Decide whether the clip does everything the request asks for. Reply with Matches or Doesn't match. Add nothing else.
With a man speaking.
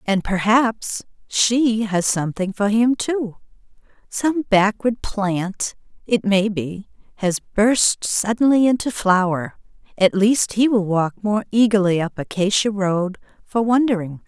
Doesn't match